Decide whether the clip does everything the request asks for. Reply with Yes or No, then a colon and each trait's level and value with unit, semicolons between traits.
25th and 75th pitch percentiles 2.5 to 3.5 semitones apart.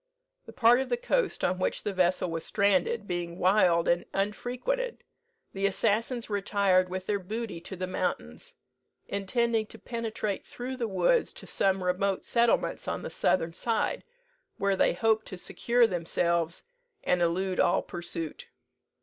No: average, 4.0 semitones